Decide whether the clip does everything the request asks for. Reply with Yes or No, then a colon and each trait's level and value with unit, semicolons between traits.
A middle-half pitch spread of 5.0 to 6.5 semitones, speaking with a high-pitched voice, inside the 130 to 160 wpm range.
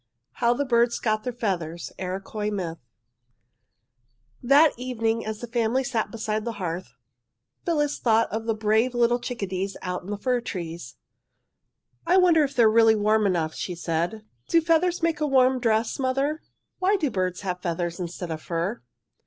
No: wide, 5.4 semitones; high, 220 Hz; average, 170 wpm